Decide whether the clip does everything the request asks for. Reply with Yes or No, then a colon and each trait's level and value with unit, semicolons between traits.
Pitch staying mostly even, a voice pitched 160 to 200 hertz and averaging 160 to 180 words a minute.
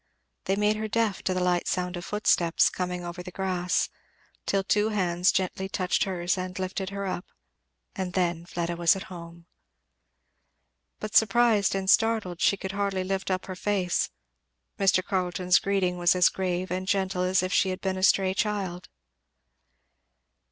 Yes: narrow, 1.6 semitones; medium, 185 Hz; average, 165 wpm